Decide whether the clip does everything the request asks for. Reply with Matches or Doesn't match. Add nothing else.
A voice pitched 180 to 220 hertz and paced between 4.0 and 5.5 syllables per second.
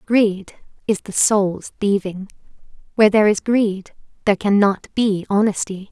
Matches